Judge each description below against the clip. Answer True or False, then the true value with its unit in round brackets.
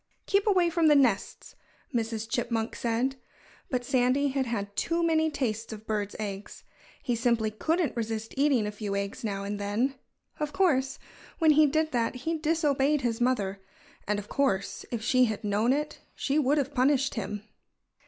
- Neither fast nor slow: True (175 wpm)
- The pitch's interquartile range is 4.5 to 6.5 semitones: True (5.0 semitones)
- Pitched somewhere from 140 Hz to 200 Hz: False (245 Hz)